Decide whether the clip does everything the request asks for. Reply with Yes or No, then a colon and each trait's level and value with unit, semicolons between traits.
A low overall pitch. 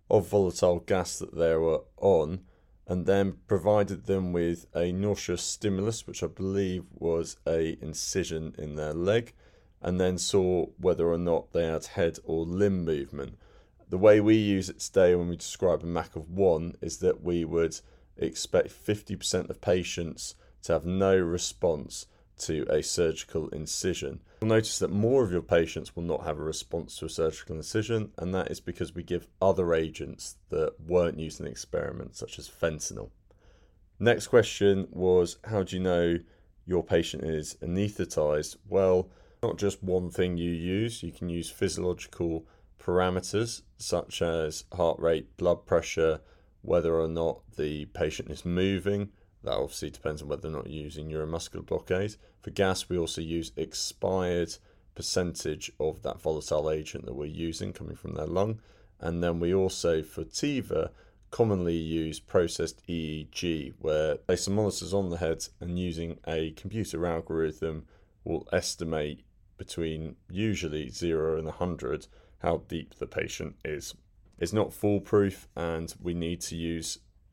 Yes: very low, 85 Hz